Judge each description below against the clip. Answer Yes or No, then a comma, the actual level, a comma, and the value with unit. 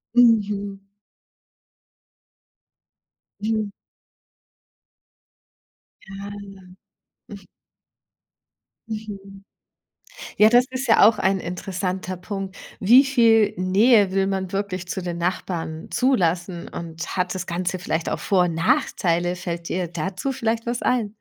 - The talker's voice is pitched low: No, high, 195 Hz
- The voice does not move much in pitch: No, average, 3.2 semitones